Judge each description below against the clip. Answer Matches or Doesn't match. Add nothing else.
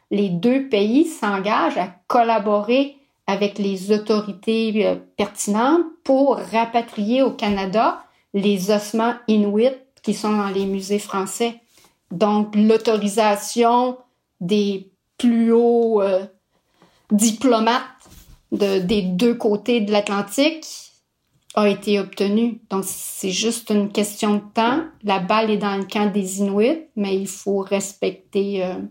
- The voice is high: Matches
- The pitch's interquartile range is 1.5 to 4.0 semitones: Matches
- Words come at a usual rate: Doesn't match